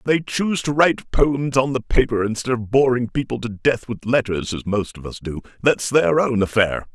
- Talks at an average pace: No, fast, 225 wpm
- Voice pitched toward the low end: Yes, low, 120 Hz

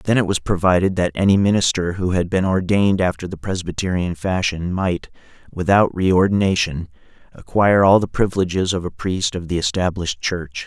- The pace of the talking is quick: No, average, 165 wpm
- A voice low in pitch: Yes, very low, 95 Hz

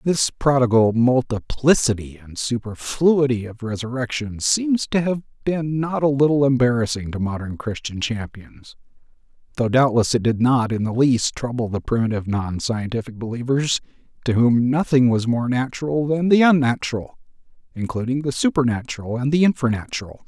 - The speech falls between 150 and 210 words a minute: No, average, 140 wpm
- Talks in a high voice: No, low, 125 Hz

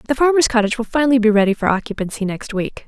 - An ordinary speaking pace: No, fast, 230 wpm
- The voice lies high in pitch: Yes, high, 230 Hz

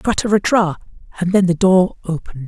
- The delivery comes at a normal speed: No, slow, 120 wpm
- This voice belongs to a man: Yes, male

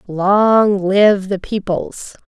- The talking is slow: Yes, slow, 105 wpm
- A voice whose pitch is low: No, high, 195 Hz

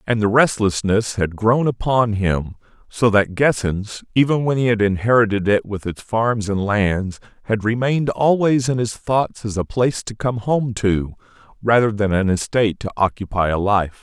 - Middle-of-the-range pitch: No, low, 110 Hz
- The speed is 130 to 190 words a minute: Yes, average, 180 wpm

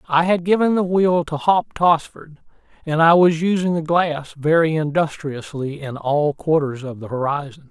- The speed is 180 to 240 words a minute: No, average, 170 wpm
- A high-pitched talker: No, medium, 155 Hz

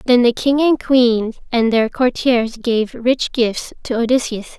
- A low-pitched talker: No, high, 240 Hz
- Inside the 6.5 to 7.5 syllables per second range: No, 3.9 syllables/s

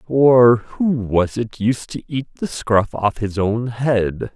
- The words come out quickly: No, average, 180 wpm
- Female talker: No, male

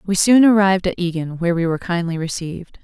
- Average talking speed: No, fast, 210 wpm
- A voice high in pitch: No, medium, 180 Hz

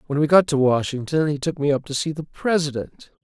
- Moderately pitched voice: Yes, medium, 145 Hz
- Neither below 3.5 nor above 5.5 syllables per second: No, 5.7 syllables/s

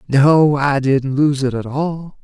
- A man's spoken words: Yes, male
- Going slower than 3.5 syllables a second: Yes, 2.9 syllables/s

